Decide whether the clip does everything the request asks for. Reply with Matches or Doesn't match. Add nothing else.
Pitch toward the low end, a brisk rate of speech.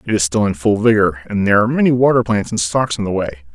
Matches